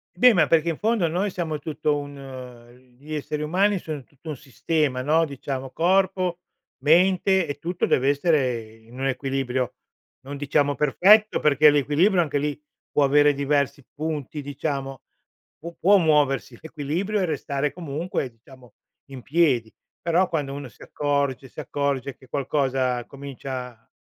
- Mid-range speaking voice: Yes, medium, 145 Hz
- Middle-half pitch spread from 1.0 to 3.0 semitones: No, average, 3.4 semitones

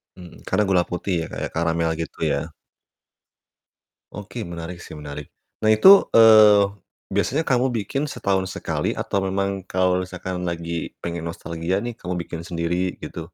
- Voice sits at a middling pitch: No, very low, 90 Hz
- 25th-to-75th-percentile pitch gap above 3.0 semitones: Yes, average, 3.4 semitones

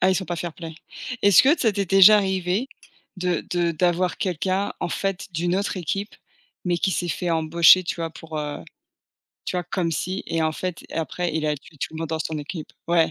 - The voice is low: No, medium, 175 Hz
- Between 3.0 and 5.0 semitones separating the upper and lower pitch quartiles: No, narrow, 2.6 semitones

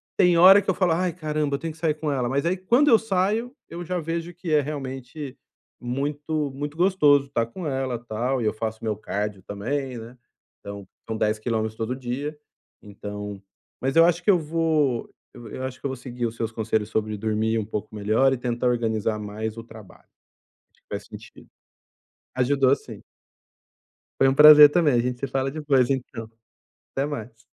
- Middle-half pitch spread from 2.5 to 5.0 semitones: No, wide, 5.4 semitones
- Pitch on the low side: Yes, low, 130 Hz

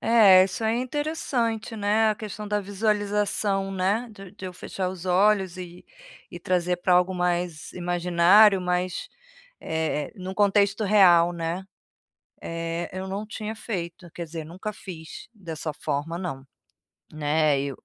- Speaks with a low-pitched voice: No, medium, 185 Hz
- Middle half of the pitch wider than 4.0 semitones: No, average, 3.3 semitones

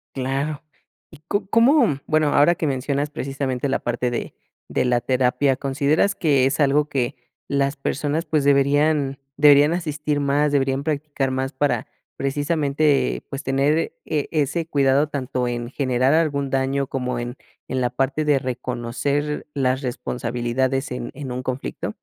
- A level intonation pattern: Yes, narrow, 2.2 semitones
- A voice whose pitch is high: No, medium, 140 Hz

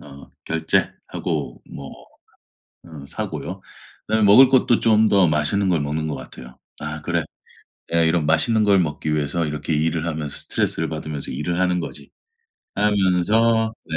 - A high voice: No, very low, 80 Hz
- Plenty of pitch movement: No, average, 4.8 semitones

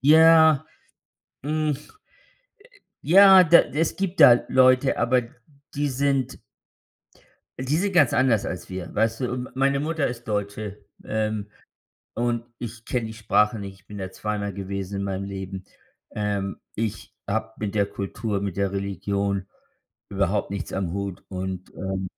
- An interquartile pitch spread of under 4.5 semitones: No, average, 5.0 semitones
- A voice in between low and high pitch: No, low, 110 Hz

